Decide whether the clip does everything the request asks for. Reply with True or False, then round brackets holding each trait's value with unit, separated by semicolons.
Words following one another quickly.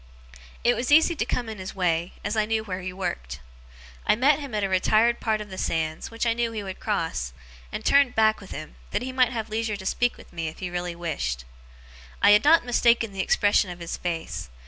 True (235 wpm)